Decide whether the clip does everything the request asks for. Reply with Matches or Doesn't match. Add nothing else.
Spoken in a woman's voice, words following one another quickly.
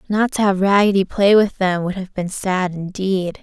Matches